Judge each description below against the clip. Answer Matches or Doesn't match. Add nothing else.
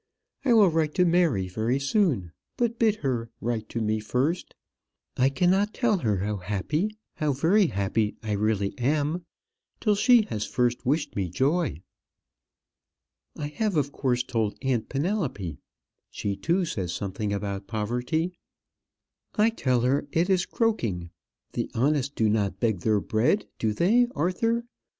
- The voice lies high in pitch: Doesn't match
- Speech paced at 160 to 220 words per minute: Doesn't match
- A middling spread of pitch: Doesn't match